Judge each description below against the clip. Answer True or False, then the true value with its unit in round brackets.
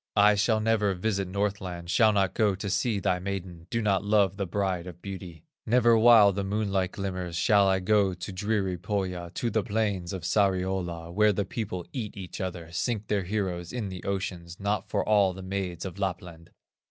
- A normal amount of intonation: False (2.3 semitones)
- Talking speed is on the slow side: False (190 wpm)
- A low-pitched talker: True (95 Hz)